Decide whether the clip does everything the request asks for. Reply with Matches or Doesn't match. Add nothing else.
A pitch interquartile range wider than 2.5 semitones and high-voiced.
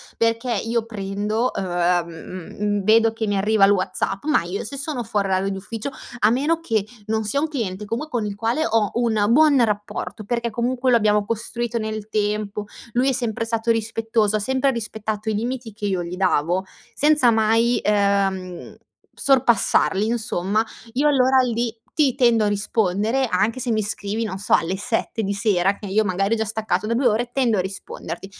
Matches